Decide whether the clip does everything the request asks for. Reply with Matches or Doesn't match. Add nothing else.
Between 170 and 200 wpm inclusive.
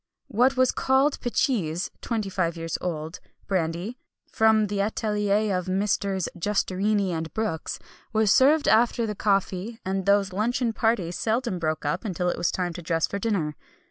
Doesn't match